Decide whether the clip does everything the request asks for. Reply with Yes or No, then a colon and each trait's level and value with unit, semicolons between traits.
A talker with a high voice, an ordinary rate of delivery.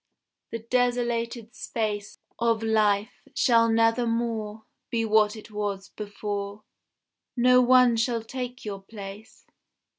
No: high, 225 Hz; slow, 110 wpm